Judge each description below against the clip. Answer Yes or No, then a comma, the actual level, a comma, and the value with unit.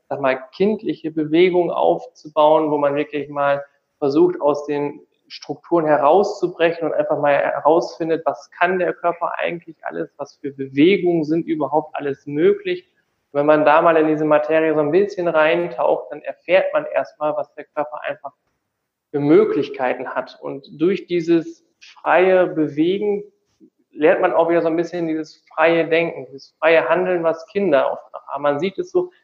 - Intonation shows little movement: No, average, 3.6 semitones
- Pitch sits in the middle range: Yes, medium, 160 Hz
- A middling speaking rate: Yes, average, 165 wpm